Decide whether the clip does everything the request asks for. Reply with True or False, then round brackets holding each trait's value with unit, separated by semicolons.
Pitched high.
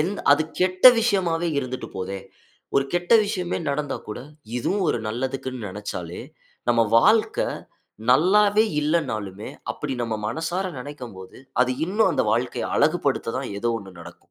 False (140 Hz)